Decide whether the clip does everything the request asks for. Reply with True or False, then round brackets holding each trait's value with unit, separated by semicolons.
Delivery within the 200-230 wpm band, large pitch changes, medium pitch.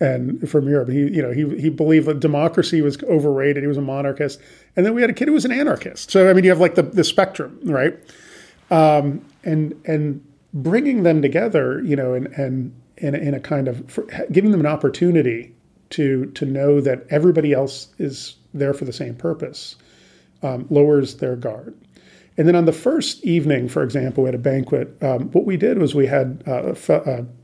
False (205 wpm; 3.2 semitones; 145 Hz)